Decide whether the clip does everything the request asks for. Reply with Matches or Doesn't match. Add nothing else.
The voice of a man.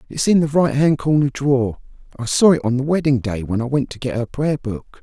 Matches